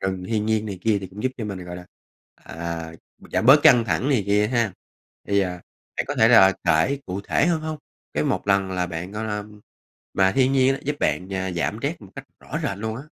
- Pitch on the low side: Yes, low, 105 Hz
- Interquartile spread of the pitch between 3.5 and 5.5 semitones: Yes, average, 4.0 semitones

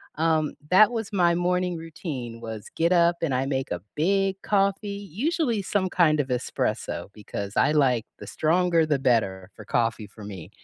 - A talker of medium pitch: Yes, medium, 160 Hz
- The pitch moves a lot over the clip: Yes, wide, 7.1 semitones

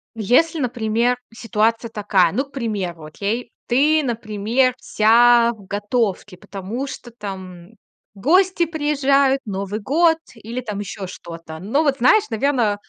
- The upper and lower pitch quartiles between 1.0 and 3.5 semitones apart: No, average, 4.8 semitones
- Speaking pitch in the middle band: No, high, 230 Hz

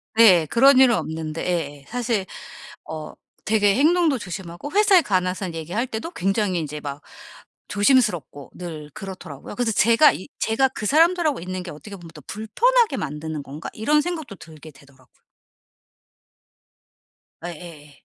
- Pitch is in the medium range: No, high, 195 Hz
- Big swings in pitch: Yes, wide, 7.7 semitones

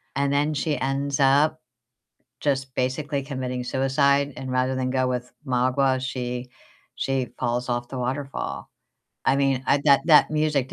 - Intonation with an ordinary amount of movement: No, narrow, 1.7 semitones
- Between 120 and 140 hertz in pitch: Yes, low, 135 Hz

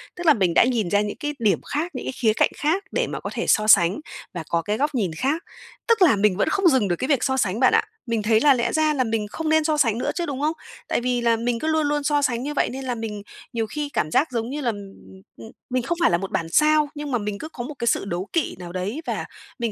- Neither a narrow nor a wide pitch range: No, wide, 5.9 semitones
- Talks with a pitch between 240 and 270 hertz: Yes, high, 245 Hz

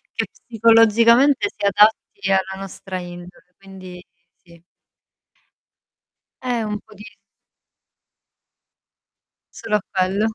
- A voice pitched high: Yes, high, 200 Hz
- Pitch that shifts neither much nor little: Yes, average, 3.3 semitones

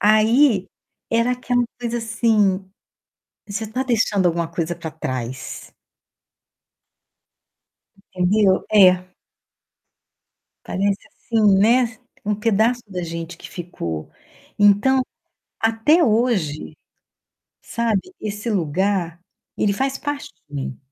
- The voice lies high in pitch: Yes, high, 205 Hz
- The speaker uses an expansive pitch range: No, average, 4.5 semitones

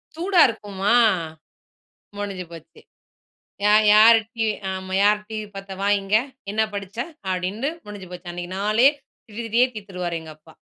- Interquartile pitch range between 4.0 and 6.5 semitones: No, average, 2.8 semitones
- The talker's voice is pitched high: Yes, high, 205 Hz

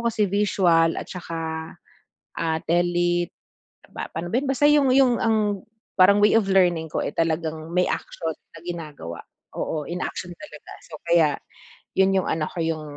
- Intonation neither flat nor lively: Yes, average, 3.6 semitones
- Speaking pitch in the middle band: Yes, medium, 175 Hz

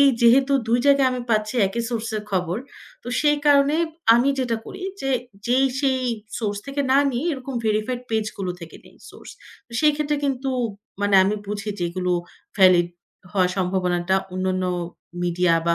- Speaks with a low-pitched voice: No, high, 220 Hz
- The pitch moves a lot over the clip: Yes, wide, 6.2 semitones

